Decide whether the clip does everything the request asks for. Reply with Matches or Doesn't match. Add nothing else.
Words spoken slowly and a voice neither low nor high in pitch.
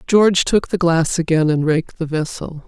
Doesn't match